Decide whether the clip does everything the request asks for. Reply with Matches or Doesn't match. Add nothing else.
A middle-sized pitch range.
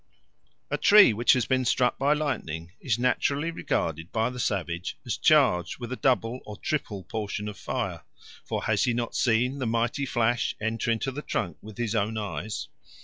Matches